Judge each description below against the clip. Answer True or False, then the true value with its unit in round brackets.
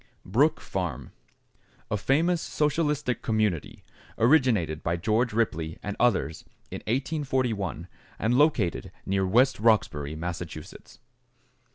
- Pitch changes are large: True (7.2 semitones)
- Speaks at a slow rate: True (100 wpm)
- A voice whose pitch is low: True (110 Hz)